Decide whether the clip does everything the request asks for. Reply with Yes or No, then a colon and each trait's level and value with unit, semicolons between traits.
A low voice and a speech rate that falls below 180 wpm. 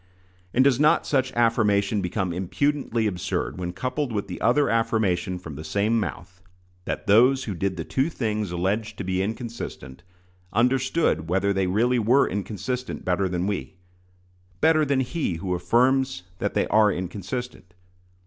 Yes: low, 105 Hz; average, 155 wpm